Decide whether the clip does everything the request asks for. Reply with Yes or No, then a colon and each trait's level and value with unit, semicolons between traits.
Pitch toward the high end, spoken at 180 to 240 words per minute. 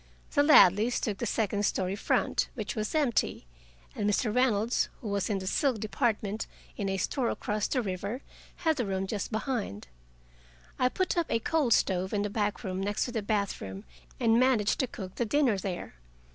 Yes: high, 215 Hz; average, 185 wpm